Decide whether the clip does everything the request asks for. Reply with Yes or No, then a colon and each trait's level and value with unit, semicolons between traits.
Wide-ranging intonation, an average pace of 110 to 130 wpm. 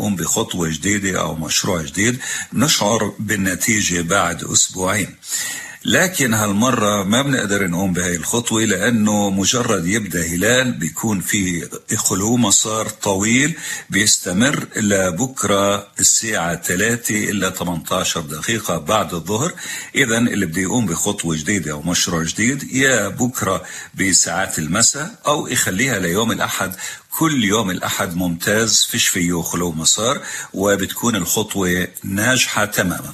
No: average, 3.6 semitones; average, 120 wpm